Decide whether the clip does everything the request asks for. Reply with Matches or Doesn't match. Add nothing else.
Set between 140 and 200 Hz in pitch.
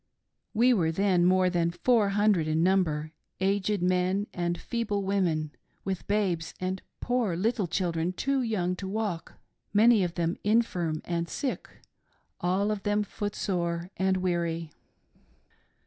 Matches